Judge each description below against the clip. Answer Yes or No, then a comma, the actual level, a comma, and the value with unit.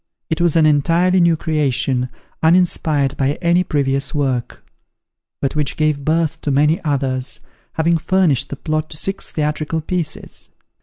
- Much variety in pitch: No, average, 2.9 semitones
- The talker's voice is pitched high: No, medium, 155 Hz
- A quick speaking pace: No, average, 145 wpm